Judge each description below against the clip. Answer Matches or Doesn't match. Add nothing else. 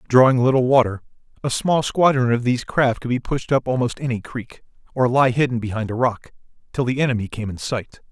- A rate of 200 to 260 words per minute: Matches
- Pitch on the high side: Doesn't match